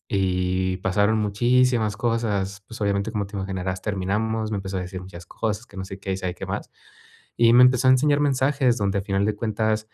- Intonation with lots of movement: No, average, 3.2 semitones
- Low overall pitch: Yes, low, 105 Hz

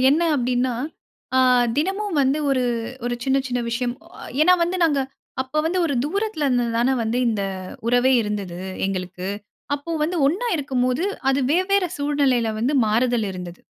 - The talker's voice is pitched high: Yes, very high, 265 Hz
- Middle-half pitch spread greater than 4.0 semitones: Yes, average, 4.4 semitones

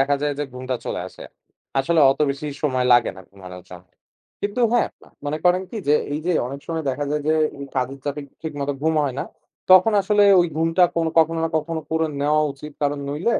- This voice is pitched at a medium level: Yes, medium, 150 Hz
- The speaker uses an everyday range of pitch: Yes, average, 3.1 semitones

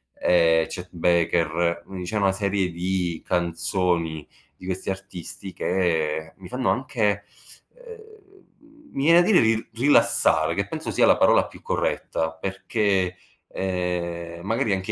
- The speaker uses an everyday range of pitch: Yes, average, 3.2 semitones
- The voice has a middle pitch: No, very low, 95 Hz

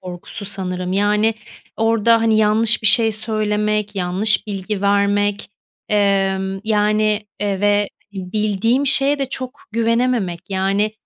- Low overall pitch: No, high, 210 Hz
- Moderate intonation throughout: No, narrow, 2.1 semitones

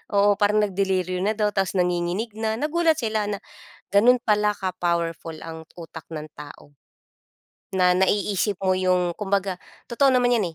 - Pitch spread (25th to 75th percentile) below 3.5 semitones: Yes, average, 3.0 semitones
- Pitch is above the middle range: Yes, high, 195 Hz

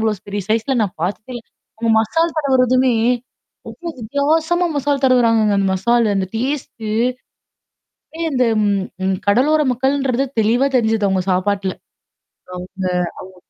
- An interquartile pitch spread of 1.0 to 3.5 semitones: No, average, 4.8 semitones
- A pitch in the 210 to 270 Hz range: Yes, high, 230 Hz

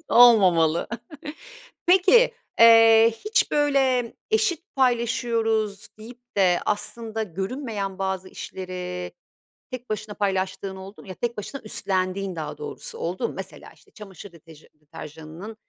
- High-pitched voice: Yes, high, 215 Hz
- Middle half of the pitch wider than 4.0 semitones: Yes, average, 4.6 semitones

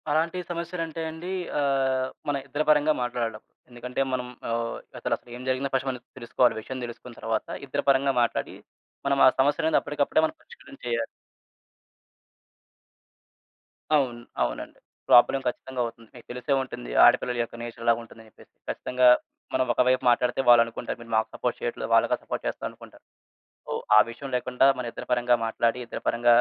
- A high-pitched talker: No, low, 125 Hz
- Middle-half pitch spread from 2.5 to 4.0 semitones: Yes, average, 2.8 semitones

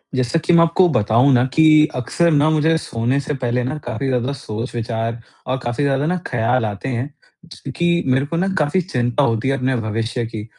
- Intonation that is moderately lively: Yes, average, 4.2 semitones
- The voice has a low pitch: Yes, low, 130 Hz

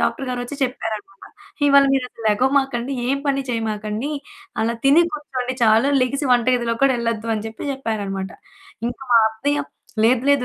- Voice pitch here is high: Yes, high, 245 Hz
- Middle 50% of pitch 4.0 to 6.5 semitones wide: No, average, 3.5 semitones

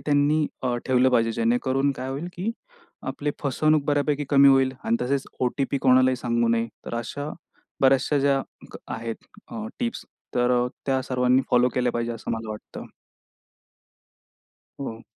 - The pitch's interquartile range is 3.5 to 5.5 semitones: No, average, 2.7 semitones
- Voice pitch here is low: Yes, low, 130 Hz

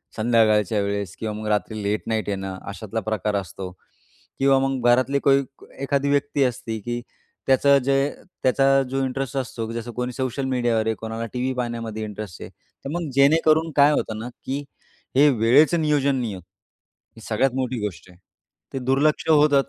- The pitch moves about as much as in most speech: Yes, average, 4.1 semitones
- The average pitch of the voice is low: Yes, low, 125 Hz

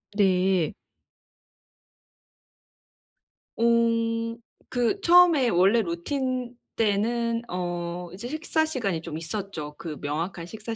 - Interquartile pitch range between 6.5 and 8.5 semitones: No, average, 5.3 semitones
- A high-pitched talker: Yes, high, 220 Hz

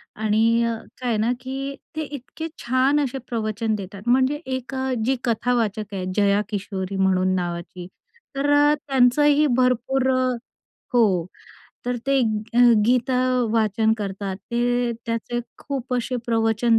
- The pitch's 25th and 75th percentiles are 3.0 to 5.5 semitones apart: Yes, average, 3.7 semitones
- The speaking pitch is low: No, high, 235 Hz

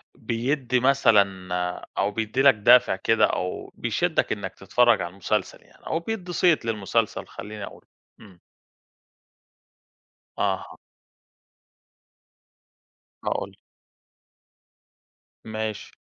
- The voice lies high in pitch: No, low, 110 Hz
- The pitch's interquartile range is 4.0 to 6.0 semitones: Yes, average, 4.4 semitones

